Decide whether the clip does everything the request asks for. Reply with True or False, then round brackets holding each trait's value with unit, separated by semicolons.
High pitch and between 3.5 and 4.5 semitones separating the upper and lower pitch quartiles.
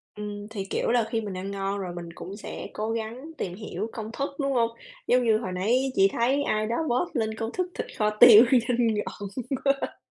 False (220 Hz; 3.1 semitones)